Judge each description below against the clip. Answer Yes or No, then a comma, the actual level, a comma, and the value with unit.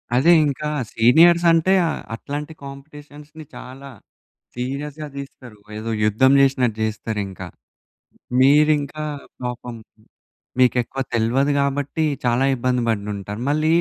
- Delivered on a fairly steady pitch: No, average, 3.9 semitones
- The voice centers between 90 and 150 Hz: Yes, low, 135 Hz